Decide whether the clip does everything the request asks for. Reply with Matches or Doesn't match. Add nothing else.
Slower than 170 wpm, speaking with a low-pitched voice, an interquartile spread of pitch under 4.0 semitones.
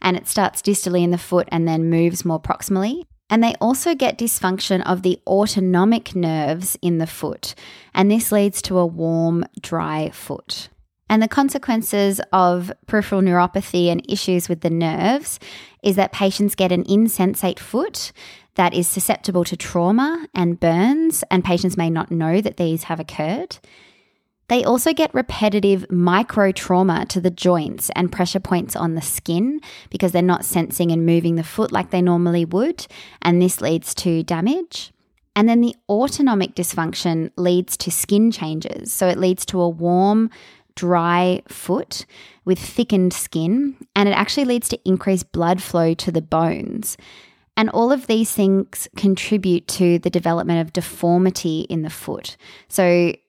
Doesn't match